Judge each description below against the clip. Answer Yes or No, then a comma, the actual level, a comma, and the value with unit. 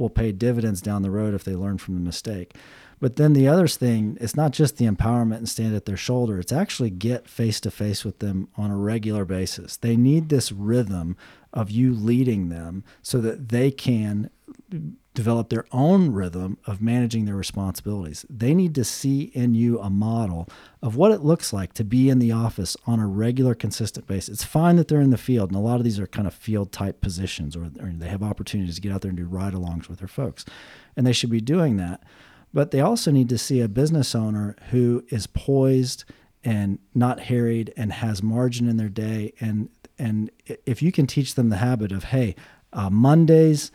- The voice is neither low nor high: No, low, 115 Hz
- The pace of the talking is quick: Yes, fast, 215 wpm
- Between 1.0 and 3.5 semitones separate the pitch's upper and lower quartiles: No, average, 4.1 semitones